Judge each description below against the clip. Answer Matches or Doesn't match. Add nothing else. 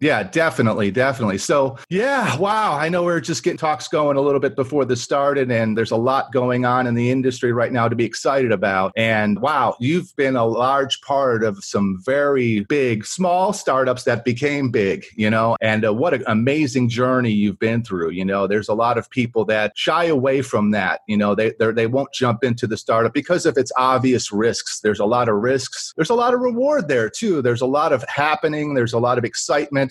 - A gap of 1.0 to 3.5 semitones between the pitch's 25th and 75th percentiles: Doesn't match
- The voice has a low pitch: Matches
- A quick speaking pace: Matches